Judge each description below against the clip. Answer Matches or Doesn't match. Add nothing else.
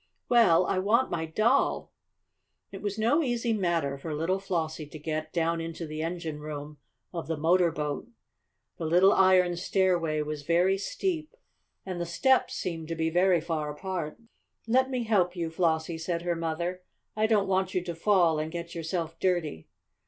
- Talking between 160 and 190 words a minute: Matches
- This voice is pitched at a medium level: Matches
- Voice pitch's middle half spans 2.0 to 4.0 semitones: Matches